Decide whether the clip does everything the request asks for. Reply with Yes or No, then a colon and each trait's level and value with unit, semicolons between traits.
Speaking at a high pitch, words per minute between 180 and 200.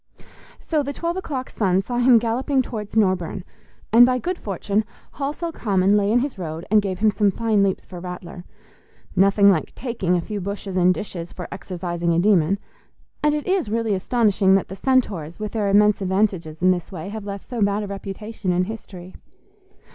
Yes: high, 200 Hz; average, 190 wpm